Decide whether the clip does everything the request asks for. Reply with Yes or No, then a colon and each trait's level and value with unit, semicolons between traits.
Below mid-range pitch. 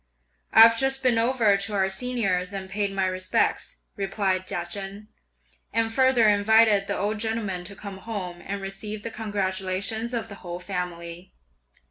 No: high, 200 Hz